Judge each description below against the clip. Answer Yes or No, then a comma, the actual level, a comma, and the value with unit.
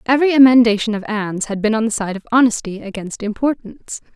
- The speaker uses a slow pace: No, average, 190 wpm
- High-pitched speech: Yes, high, 225 Hz